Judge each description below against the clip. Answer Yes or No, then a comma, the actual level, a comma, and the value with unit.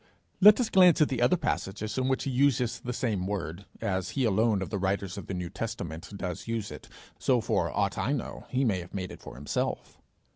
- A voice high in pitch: No, low, 105 Hz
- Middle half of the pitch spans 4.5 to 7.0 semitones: Yes, wide, 5.4 semitones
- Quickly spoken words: Yes, fast, 225 wpm